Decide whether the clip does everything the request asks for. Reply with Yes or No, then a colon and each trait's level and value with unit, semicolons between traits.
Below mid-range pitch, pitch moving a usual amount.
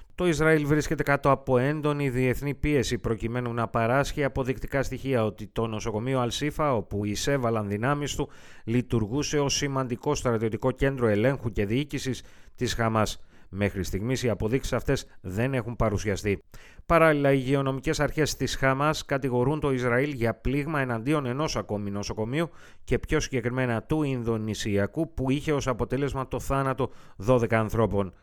Yes: low, 130 Hz; average, 3.8 semitones